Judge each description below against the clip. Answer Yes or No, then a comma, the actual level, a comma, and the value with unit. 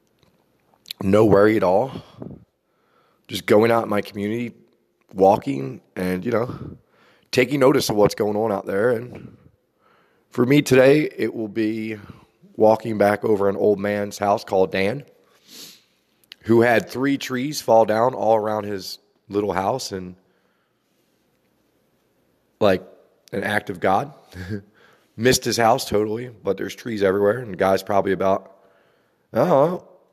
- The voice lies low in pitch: Yes, low, 105 Hz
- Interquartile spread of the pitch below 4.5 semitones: Yes, average, 3.0 semitones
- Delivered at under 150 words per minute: Yes, average, 140 wpm